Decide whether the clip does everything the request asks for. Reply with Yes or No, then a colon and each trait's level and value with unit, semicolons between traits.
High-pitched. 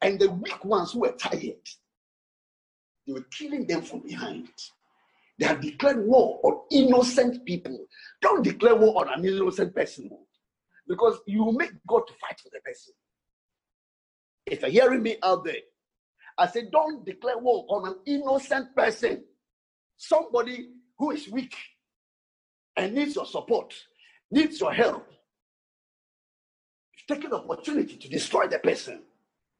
Yes: very high, 265 Hz